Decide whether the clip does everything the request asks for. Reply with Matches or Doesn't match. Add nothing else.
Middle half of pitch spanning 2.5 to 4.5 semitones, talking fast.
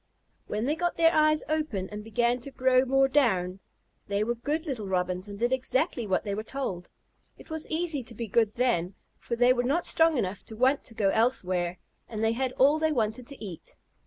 Doesn't match